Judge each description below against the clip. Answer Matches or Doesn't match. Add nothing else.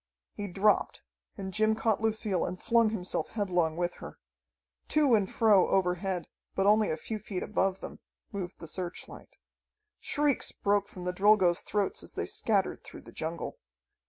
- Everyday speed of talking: Matches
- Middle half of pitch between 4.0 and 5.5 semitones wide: Doesn't match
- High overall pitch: Matches